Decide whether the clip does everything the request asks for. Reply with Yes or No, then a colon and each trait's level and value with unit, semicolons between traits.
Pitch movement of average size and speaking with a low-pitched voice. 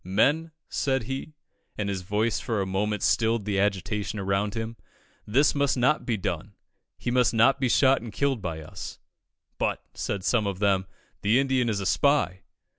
Yes: average, 4.5 semitones; low, 110 Hz